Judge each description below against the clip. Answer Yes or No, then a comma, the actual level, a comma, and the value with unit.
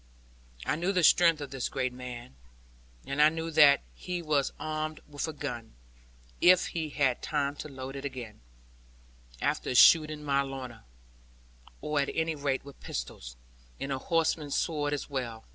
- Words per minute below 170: Yes, average, 160 wpm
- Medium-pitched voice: Yes, medium, 145 Hz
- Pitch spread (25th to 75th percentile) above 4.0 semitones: No, average, 2.9 semitones